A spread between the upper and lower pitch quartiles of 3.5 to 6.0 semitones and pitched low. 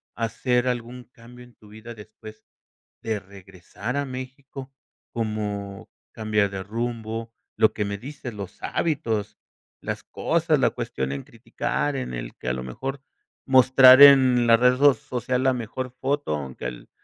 Yes: average, 3.9 semitones; low, 115 Hz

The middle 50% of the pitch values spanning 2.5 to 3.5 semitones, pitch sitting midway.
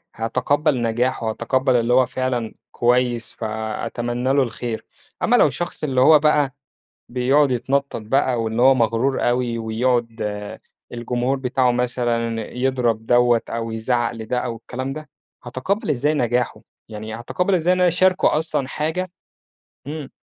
No: average, 2.8 semitones; low, 125 Hz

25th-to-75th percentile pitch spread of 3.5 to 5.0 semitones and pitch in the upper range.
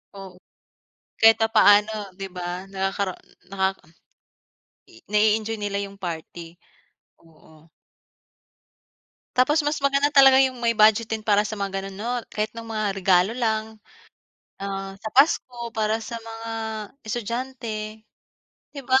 No: average, 3.0 semitones; high, 215 Hz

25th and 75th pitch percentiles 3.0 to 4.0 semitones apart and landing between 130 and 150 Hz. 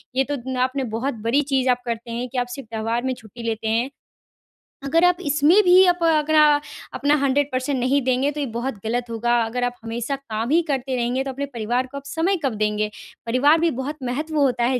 No: average, 3.3 semitones; very high, 260 Hz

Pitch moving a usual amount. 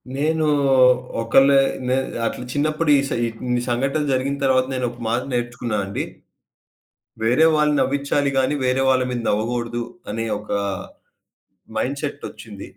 Yes: average, 3.0 semitones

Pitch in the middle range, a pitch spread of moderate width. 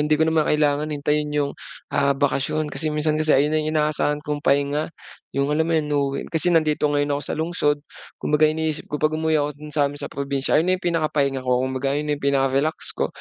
No: medium, 150 Hz; narrow, 1.5 semitones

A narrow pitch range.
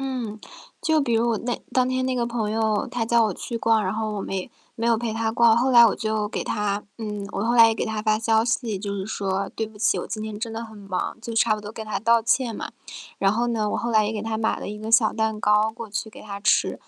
Yes: narrow, 1.7 semitones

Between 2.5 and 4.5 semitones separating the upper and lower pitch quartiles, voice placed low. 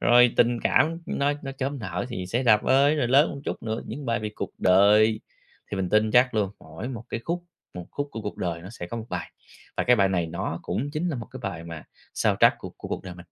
No: wide, 5.5 semitones; low, 115 Hz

